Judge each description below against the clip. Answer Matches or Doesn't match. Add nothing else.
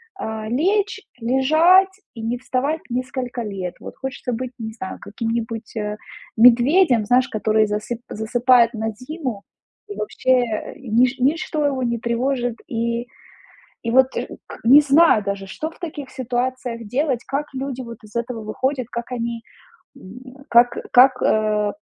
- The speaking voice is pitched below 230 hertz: Doesn't match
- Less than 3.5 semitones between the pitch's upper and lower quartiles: Matches